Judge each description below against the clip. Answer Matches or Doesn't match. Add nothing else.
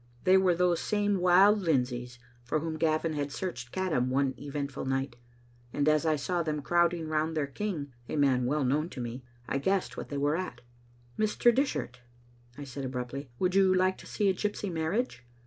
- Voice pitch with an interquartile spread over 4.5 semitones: Matches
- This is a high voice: Doesn't match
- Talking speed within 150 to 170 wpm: Doesn't match